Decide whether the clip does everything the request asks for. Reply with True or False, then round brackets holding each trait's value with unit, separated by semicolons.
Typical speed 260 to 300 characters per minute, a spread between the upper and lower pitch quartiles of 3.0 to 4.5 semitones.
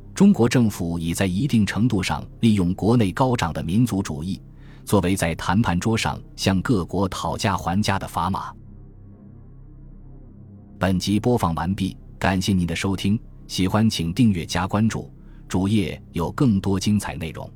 False (230 characters per minute; 3.6 semitones)